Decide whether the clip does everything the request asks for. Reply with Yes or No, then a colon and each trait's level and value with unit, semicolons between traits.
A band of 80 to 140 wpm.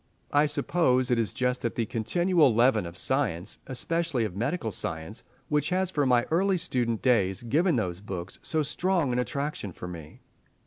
No: average, 170 wpm